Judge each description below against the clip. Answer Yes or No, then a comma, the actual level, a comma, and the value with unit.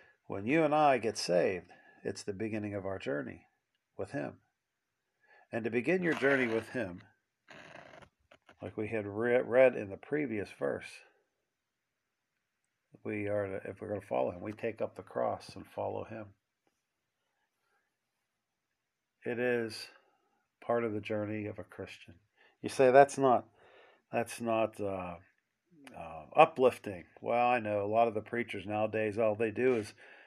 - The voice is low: Yes, low, 115 Hz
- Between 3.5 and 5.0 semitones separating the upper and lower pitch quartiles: No, average, 2.9 semitones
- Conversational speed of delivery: Yes, average, 150 wpm